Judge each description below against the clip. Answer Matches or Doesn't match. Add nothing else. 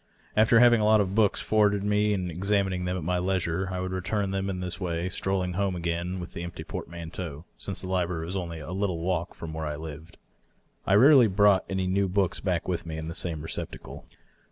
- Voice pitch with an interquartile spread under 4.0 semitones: Matches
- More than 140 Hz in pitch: Doesn't match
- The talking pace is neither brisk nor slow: Doesn't match